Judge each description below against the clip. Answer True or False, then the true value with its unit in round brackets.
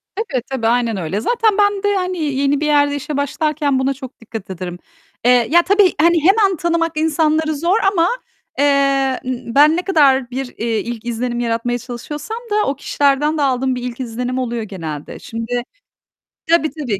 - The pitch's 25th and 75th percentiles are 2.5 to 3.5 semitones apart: False (4.9 semitones)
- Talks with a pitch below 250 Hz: False (275 Hz)